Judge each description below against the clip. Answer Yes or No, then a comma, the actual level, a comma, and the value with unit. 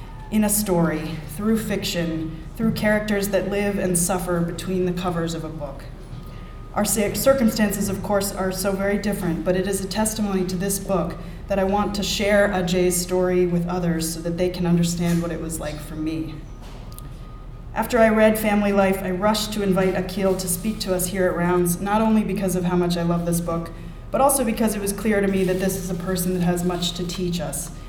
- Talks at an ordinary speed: No, fast, 215 wpm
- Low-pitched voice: No, medium, 185 Hz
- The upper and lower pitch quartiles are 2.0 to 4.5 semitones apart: Yes, average, 2.8 semitones